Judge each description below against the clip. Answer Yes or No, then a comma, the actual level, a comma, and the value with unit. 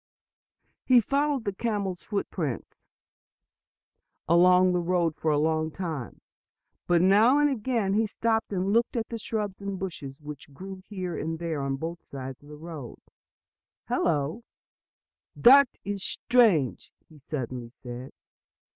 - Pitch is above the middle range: No, medium, 180 Hz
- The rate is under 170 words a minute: Yes, average, 140 wpm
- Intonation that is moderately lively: No, wide, 6.0 semitones